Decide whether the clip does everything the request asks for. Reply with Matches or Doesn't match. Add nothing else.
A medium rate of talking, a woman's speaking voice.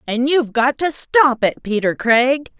Matches